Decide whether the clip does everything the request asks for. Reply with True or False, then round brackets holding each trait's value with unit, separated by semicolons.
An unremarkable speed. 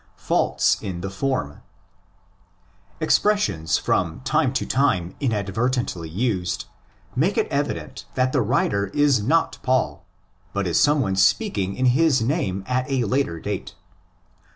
False (130 wpm)